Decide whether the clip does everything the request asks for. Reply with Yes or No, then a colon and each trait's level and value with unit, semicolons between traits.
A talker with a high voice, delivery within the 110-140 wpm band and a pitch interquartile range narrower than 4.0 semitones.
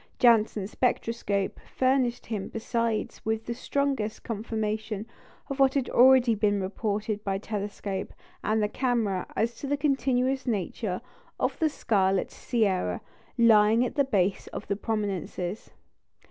Yes: high, 220 Hz; slow, 135 wpm; average, 3.4 semitones